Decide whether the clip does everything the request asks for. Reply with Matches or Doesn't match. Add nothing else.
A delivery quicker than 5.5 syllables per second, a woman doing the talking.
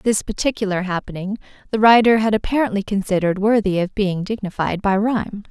Matches